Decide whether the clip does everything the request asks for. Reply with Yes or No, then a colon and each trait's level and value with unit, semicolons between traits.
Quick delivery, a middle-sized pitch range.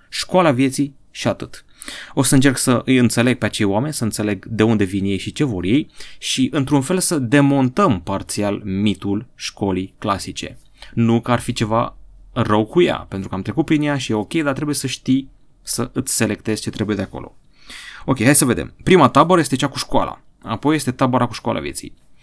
Yes: fast, 205 wpm; average, 4.7 semitones